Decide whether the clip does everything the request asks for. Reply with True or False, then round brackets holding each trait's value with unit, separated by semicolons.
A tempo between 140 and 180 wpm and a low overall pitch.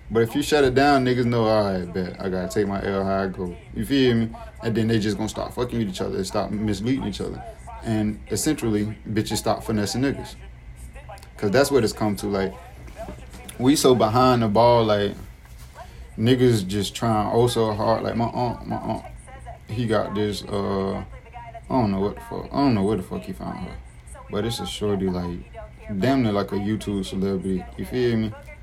False (205 wpm; 105 Hz)